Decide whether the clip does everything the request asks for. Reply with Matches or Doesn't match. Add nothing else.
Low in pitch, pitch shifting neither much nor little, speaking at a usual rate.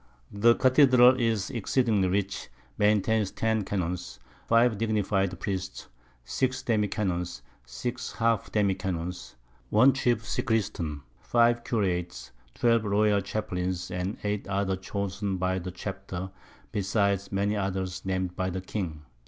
Doesn't match